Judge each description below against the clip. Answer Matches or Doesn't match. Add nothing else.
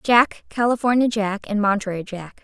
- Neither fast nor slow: Matches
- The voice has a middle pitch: Doesn't match